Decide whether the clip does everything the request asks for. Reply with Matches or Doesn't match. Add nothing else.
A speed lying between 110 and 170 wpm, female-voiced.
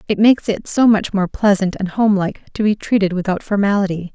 Doesn't match